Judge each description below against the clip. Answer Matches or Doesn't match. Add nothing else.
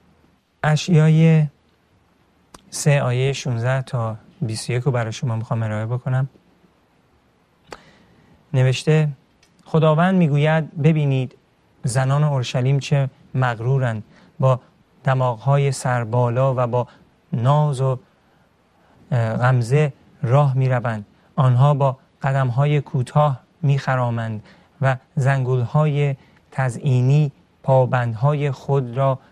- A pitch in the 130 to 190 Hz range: Matches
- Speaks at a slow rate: Matches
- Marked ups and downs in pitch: Doesn't match